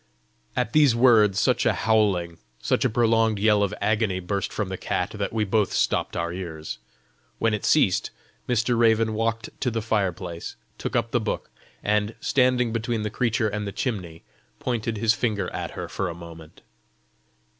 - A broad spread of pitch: No, average, 3.2 semitones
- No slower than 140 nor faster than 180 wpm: Yes, average, 175 wpm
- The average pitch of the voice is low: Yes, low, 105 Hz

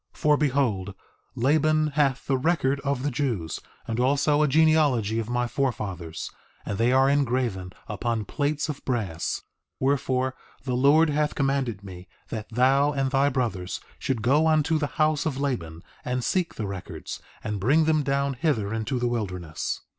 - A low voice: Yes, low, 130 Hz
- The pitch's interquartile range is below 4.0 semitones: No, average, 4.4 semitones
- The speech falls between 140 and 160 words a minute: No, average, 170 wpm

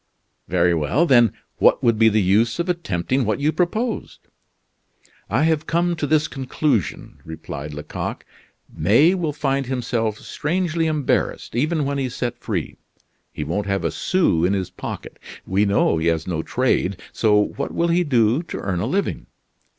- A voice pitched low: Yes, low, 125 Hz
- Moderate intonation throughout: No, wide, 8.0 semitones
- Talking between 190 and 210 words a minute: No, average, 165 wpm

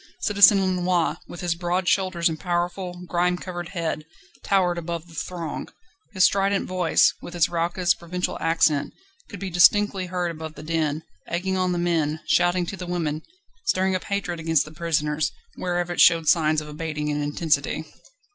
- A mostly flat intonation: Yes, narrow, 2.1 semitones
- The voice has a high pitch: No, medium, 175 Hz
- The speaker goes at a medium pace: Yes, average, 170 wpm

